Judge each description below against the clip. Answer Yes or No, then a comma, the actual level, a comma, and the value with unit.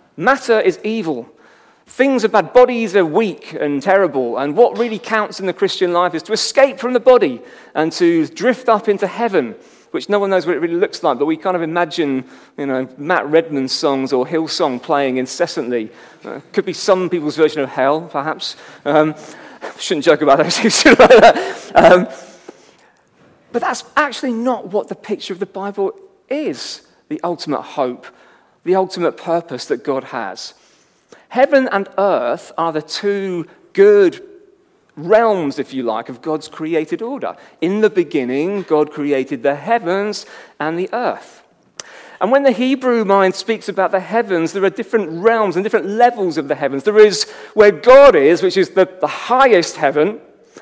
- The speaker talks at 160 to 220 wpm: Yes, average, 170 wpm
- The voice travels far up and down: Yes, wide, 6.8 semitones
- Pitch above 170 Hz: Yes, high, 190 Hz